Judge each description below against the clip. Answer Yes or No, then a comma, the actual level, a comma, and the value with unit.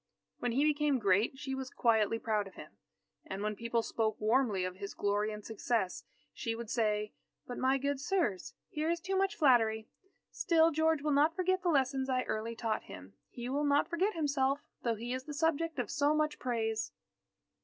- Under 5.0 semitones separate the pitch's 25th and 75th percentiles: No, average, 5.3 semitones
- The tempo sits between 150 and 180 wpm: No, average, 195 wpm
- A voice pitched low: No, very high, 255 Hz